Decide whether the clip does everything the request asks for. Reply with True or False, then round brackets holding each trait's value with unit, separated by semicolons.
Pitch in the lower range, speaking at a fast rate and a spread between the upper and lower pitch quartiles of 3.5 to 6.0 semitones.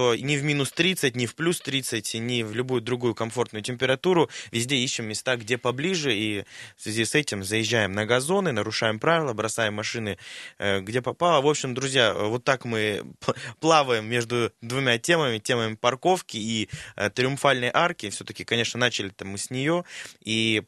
True (120 Hz; 165 wpm; 3.8 semitones)